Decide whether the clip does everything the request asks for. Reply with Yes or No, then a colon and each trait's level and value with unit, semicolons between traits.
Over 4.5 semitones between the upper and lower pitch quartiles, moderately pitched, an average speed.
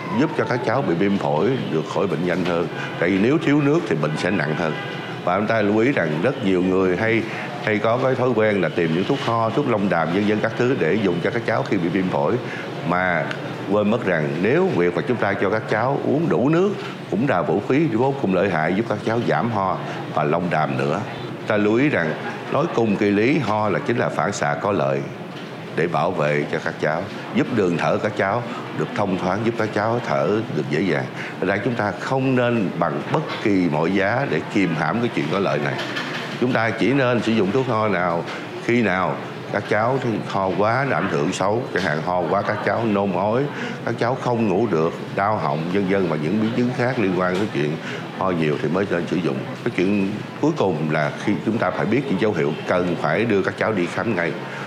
No: average, 5.2 semitones; low, 105 Hz; average, 240 wpm